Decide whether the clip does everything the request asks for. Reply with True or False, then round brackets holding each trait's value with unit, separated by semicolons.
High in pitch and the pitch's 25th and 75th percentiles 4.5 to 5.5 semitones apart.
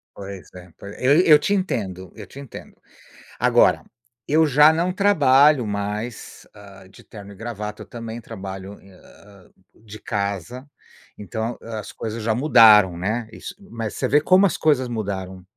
False (110 Hz; 5.2 semitones)